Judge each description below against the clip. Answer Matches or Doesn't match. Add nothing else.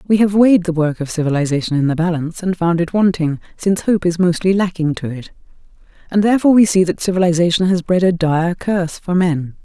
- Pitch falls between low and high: Matches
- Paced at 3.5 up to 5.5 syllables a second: Doesn't match